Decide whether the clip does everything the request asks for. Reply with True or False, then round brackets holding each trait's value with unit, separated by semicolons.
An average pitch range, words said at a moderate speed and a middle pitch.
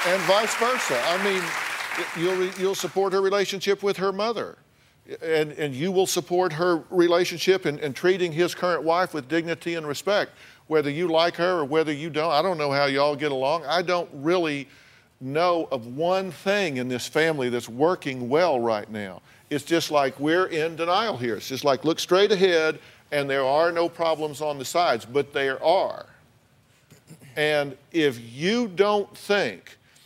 True (4.1 semitones; 180 wpm; 160 Hz)